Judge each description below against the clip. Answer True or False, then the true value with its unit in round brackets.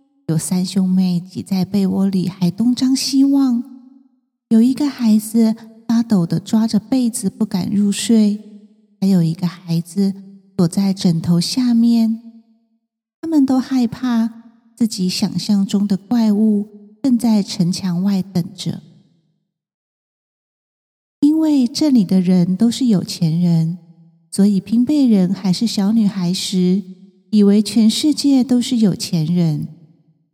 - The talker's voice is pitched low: False (205 Hz)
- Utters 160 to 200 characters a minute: True (185 characters per minute)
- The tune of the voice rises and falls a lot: False (4.1 semitones)